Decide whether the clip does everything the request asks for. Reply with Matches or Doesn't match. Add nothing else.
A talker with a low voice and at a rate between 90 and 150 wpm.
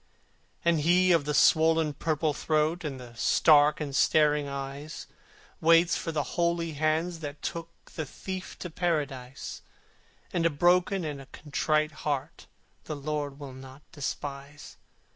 Doesn't match